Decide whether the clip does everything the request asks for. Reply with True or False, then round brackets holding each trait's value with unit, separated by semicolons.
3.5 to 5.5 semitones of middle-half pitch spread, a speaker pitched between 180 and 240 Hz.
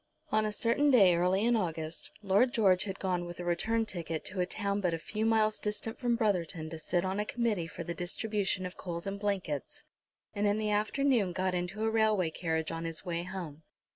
True (3.8 semitones; 190 Hz)